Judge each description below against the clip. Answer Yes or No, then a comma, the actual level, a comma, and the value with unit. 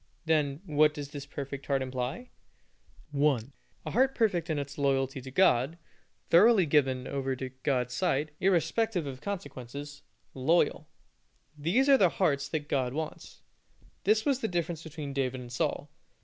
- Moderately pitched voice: Yes, medium, 145 Hz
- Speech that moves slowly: No, average, 150 wpm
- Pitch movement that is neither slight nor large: Yes, average, 4.4 semitones